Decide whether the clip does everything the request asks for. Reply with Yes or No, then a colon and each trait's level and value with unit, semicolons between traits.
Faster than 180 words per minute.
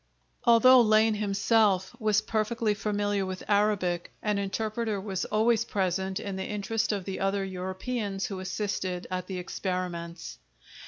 No: average, 140 wpm